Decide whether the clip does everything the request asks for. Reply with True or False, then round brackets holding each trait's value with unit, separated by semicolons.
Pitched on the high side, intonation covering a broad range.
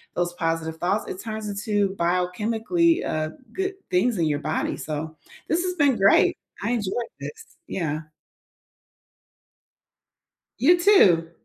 True (200 Hz; 7.1 semitones)